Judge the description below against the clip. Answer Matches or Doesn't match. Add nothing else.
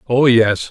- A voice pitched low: Matches